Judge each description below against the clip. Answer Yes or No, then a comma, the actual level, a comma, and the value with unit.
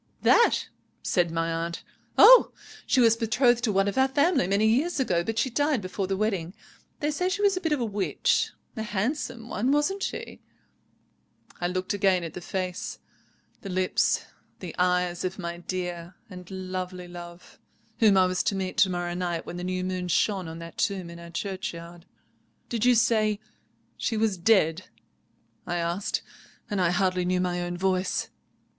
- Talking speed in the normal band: Yes, average, 180 wpm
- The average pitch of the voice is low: No, medium, 185 Hz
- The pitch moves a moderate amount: Yes, average, 4.1 semitones